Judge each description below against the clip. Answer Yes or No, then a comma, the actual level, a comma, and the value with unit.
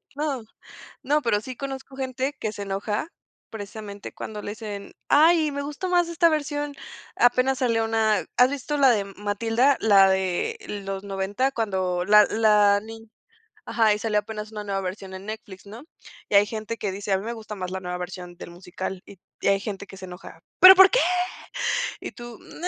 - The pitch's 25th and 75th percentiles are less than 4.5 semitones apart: No, average, 4.8 semitones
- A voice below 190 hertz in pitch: No, high, 215 Hz